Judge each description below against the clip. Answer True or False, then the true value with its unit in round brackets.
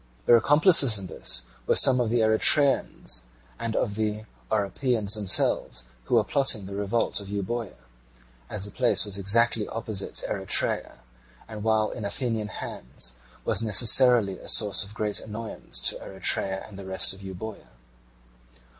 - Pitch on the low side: True (105 Hz)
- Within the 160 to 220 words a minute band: False (150 wpm)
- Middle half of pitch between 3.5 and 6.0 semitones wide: False (2.8 semitones)